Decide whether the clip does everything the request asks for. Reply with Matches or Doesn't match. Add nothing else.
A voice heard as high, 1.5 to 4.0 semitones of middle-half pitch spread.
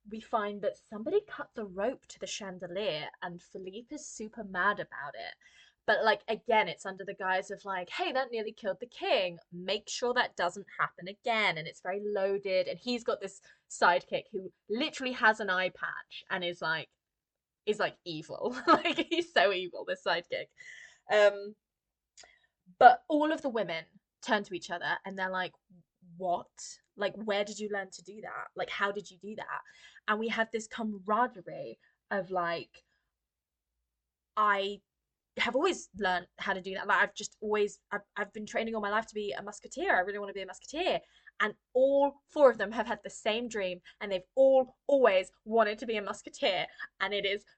Matches